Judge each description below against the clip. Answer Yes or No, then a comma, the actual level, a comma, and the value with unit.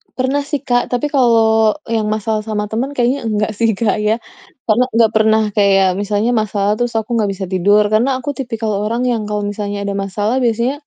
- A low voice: No, high, 220 Hz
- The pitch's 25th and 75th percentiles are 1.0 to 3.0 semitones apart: Yes, narrow, 2.6 semitones